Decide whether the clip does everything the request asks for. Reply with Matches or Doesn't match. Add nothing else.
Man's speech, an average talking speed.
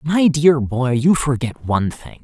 Matches